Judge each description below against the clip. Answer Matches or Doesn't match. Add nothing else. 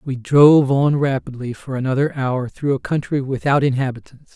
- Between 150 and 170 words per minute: Matches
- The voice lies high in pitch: Doesn't match